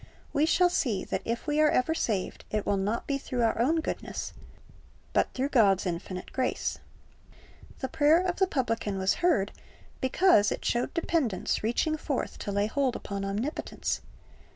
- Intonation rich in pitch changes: Yes, wide, 7.1 semitones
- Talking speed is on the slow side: No, average, 165 wpm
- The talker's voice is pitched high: Yes, very high, 250 Hz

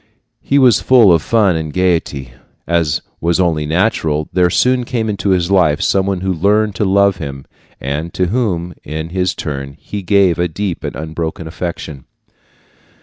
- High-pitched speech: No, very low, 90 Hz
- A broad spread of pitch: No, average, 3.9 semitones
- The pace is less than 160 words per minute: No, average, 170 wpm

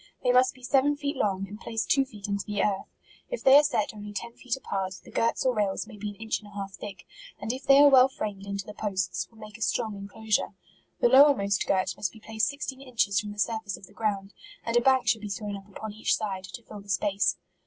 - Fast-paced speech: Yes, fast, 260 wpm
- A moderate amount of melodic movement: Yes, average, 3.7 semitones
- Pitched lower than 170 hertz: No, high, 215 Hz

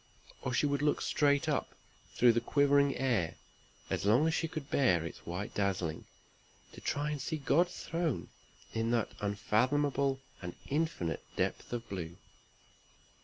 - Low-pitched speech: Yes, low, 130 Hz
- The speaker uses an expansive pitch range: Yes, wide, 6.1 semitones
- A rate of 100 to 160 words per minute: Yes, average, 150 wpm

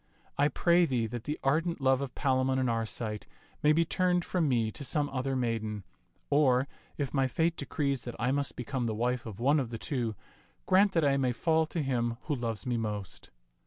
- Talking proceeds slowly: No, fast, 205 wpm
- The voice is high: No, low, 130 Hz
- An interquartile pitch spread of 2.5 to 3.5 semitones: No, average, 3.9 semitones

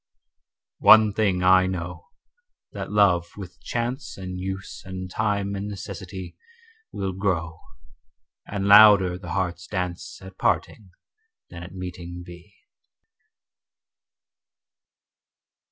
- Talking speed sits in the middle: No, slow, 105 wpm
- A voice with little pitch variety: Yes, narrow, 2.1 semitones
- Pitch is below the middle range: Yes, very low, 95 Hz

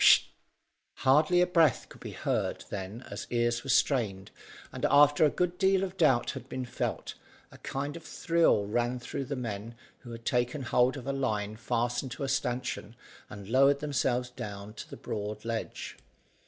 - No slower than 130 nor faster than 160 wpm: No, average, 180 wpm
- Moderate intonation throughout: Yes, average, 3.7 semitones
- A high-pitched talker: No, low, 125 Hz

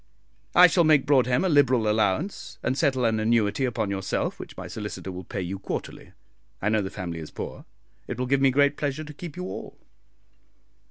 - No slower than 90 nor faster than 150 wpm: No, average, 200 wpm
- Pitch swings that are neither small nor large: No, wide, 6.3 semitones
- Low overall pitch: Yes, low, 125 Hz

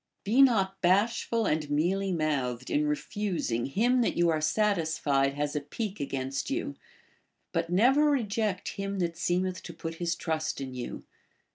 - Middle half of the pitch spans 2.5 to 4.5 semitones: No, wide, 5.4 semitones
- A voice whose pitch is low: No, medium, 175 Hz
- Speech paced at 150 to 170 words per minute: Yes, average, 160 wpm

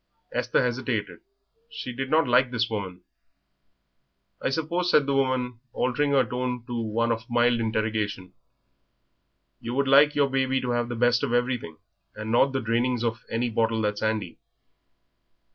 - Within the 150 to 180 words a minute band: Yes, average, 160 wpm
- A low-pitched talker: Yes, low, 120 Hz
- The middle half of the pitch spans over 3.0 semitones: No, average, 2.7 semitones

